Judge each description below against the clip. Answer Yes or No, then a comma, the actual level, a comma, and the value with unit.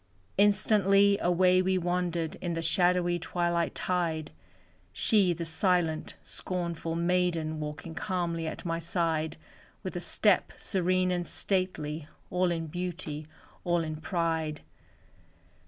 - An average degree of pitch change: No, narrow, 1.9 semitones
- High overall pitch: No, medium, 175 Hz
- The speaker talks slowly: Yes, slow, 120 wpm